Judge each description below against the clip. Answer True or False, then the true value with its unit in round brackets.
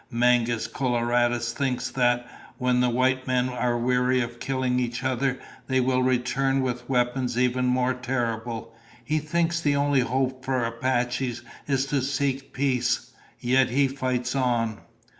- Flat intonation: True (1.5 semitones)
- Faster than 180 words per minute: False (145 wpm)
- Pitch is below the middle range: True (125 Hz)